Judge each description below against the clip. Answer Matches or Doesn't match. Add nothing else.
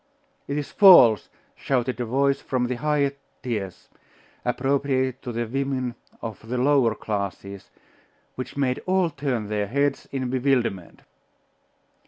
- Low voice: Matches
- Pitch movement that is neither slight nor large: Matches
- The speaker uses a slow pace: Matches